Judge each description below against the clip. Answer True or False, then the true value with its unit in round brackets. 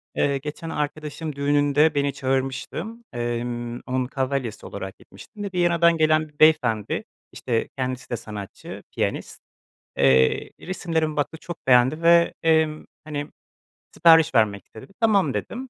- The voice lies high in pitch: False (145 Hz)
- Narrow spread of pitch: False (4.7 semitones)